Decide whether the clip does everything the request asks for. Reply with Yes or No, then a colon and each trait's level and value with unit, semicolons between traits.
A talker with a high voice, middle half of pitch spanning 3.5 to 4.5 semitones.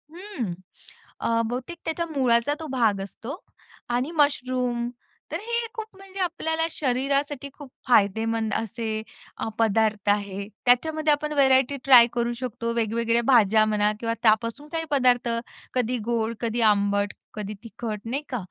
Yes: high, 240 Hz; average, 4.2 semitones